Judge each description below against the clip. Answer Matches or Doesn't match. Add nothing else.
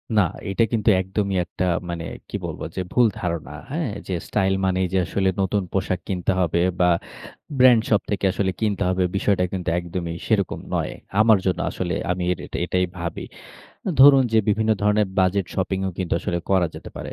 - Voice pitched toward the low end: Matches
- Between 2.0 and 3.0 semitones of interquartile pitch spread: Matches